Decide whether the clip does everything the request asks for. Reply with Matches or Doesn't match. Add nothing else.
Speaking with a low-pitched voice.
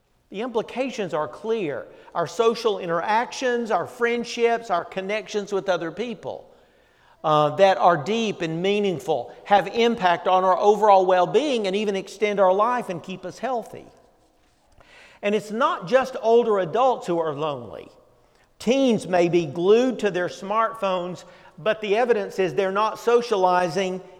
Doesn't match